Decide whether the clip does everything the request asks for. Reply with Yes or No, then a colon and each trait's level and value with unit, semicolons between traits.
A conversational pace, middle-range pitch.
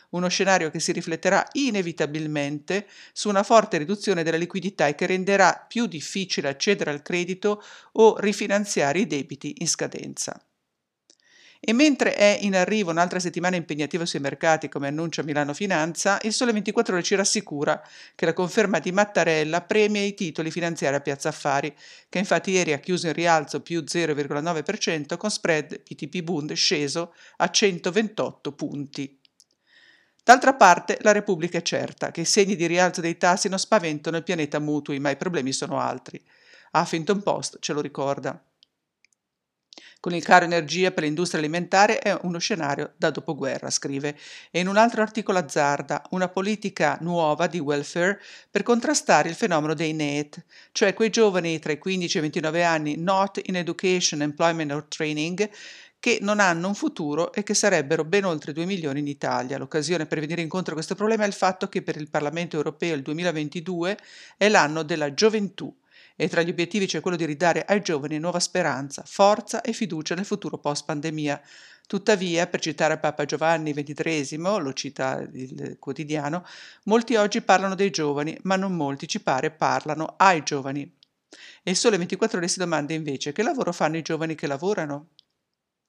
Yes: average, 165 wpm; medium, 175 Hz